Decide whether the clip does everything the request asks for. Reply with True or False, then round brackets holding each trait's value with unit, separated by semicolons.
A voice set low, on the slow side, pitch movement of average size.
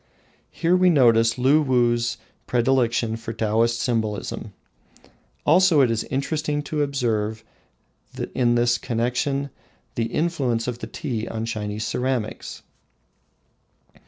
True (120 Hz; 100 wpm; 3.4 semitones)